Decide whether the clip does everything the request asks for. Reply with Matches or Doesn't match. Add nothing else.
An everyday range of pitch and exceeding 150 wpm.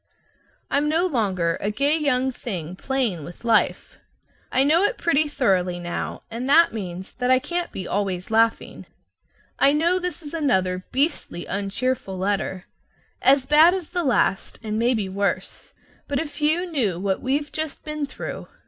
Doesn't match